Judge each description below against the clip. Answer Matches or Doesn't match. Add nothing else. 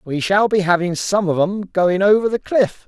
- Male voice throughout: Matches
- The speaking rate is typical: Doesn't match